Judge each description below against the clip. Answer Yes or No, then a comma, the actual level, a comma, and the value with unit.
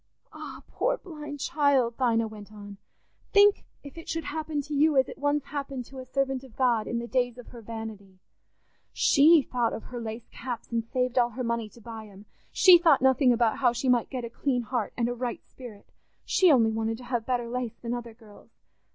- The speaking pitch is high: Yes, high, 245 Hz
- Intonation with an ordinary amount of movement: Yes, average, 3.3 semitones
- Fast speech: Yes, fast, 210 wpm